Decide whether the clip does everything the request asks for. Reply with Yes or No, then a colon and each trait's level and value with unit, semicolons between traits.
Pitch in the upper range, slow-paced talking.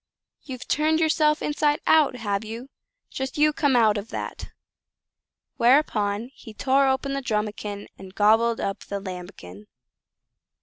Yes: high, 235 Hz; slow, 125 wpm